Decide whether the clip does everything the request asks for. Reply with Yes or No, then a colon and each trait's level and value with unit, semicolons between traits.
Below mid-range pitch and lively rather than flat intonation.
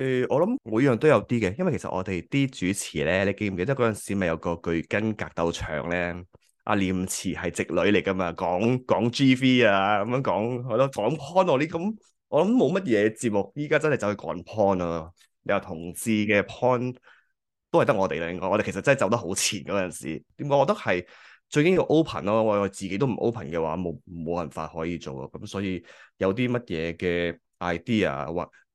Yes: low, 100 Hz; wide, 6.0 semitones